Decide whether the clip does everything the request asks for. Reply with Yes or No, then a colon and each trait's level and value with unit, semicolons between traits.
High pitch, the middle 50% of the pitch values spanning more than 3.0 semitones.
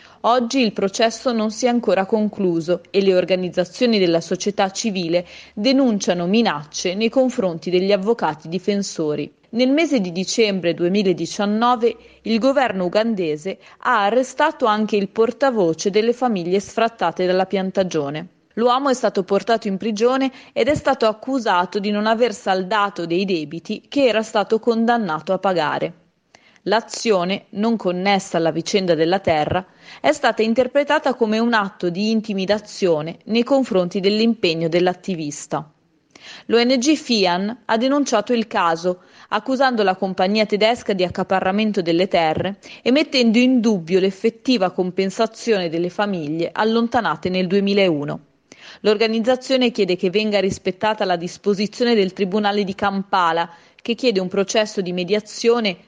Yes: high, 205 Hz; average, 3.9 semitones